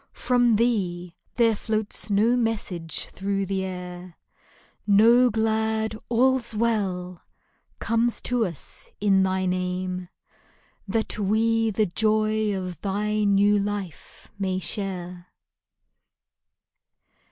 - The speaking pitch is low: No, high, 205 Hz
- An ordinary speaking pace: No, slow, 105 wpm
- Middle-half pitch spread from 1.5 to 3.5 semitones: Yes, average, 3.1 semitones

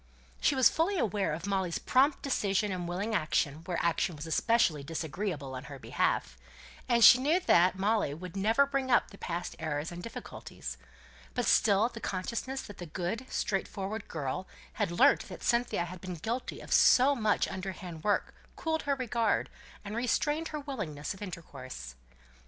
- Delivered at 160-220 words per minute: Yes, average, 165 wpm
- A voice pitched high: Yes, high, 195 Hz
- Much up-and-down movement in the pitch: Yes, wide, 5.9 semitones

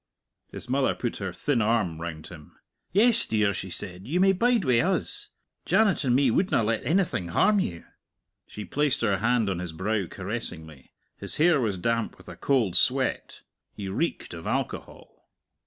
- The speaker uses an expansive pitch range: Yes, wide, 7.5 semitones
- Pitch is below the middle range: Yes, low, 115 Hz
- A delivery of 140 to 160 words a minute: No, average, 170 wpm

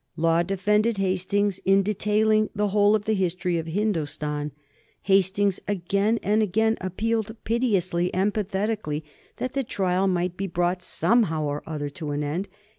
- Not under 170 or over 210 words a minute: No, average, 150 wpm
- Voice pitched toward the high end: Yes, high, 195 Hz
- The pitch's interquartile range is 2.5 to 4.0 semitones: Yes, average, 3.3 semitones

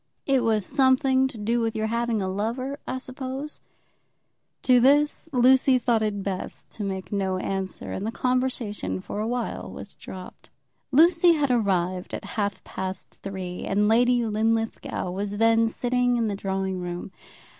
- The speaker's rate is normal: Yes, average, 165 wpm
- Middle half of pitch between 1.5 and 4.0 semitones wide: No, average, 4.5 semitones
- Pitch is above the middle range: Yes, high, 225 Hz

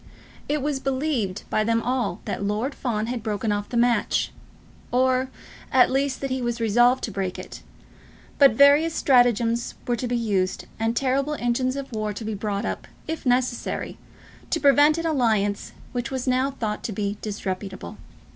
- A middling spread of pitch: Yes, average, 3.7 semitones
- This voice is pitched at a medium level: No, high, 240 Hz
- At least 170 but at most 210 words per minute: Yes, average, 175 wpm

